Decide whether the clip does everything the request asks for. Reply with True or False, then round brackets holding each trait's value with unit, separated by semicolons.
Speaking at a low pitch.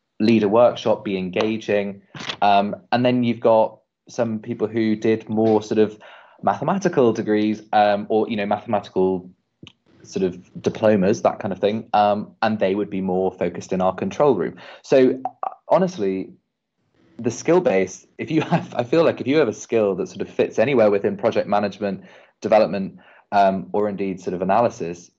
True (105 Hz)